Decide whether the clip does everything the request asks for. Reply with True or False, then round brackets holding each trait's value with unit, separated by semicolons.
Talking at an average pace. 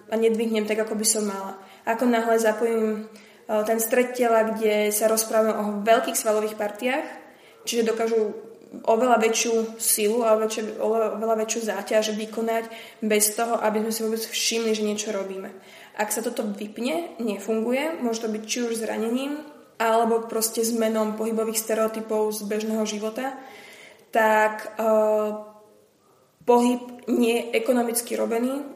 True (140 wpm)